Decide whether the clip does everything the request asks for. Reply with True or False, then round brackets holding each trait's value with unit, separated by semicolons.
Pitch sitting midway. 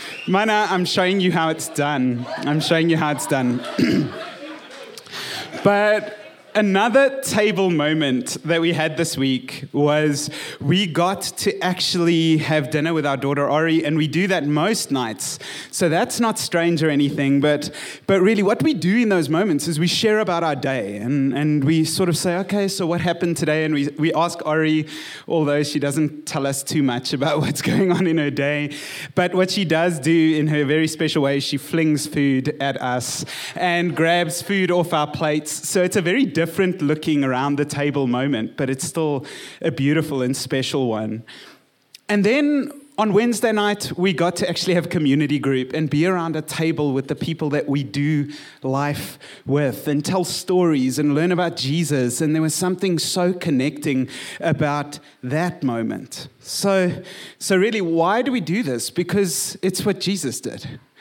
True (160 Hz)